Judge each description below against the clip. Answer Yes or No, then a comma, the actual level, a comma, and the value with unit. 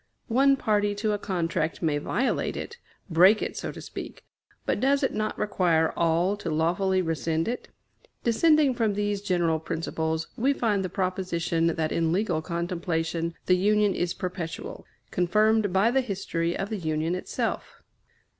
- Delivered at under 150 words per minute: No, average, 155 wpm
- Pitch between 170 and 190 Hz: Yes, medium, 185 Hz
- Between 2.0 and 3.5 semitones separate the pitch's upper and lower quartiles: No, average, 4.2 semitones